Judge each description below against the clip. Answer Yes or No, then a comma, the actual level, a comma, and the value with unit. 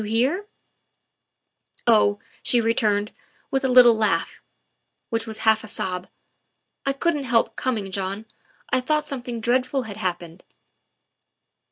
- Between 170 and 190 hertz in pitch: No, high, 230 Hz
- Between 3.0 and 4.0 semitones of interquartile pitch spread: Yes, average, 3.7 semitones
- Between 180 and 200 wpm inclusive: No, average, 140 wpm